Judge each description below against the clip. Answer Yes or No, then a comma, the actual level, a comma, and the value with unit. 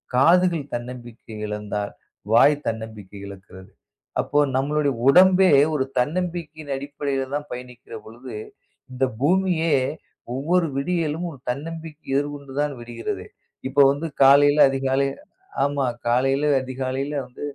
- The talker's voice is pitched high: No, medium, 140 Hz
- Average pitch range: Yes, average, 3.3 semitones